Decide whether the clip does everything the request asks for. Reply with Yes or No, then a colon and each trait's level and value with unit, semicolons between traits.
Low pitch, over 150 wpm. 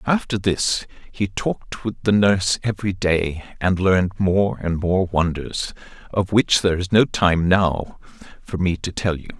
Yes: very low, 95 Hz; average, 170 wpm